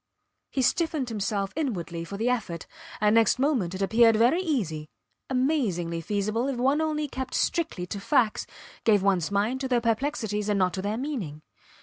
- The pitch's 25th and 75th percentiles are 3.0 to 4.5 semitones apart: No, average, 5.1 semitones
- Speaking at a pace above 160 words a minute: Yes, average, 170 wpm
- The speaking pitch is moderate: No, high, 225 Hz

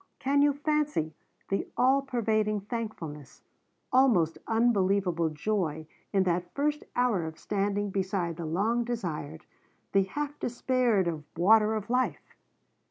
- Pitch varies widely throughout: Yes, wide, 5.9 semitones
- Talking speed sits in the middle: No, slow, 125 wpm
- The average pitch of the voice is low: No, high, 205 Hz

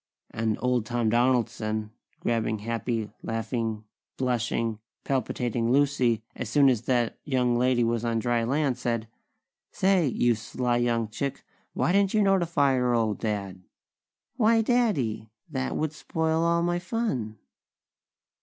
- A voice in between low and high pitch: No, low, 120 Hz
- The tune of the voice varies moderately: Yes, average, 4.0 semitones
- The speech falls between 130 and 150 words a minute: Yes, slow, 135 wpm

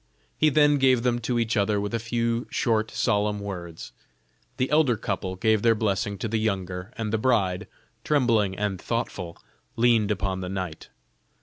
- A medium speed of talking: Yes, average, 170 wpm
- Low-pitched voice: Yes, low, 110 Hz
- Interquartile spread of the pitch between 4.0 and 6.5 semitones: No, average, 3.2 semitones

